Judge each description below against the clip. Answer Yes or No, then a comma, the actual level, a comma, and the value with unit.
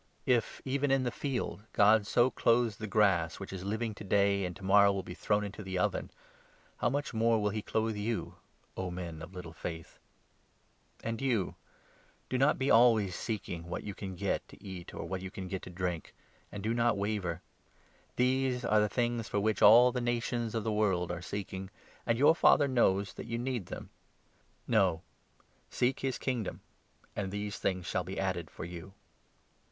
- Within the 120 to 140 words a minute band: No, average, 200 wpm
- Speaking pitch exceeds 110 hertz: No, low, 105 Hz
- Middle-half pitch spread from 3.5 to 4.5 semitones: Yes, average, 3.9 semitones